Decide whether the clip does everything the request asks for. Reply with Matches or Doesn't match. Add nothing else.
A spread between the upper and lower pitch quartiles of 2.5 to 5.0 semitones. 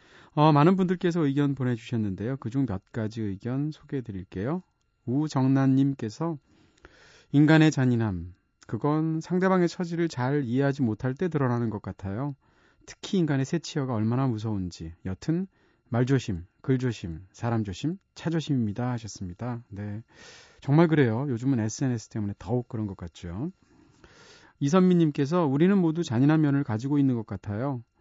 Doesn't match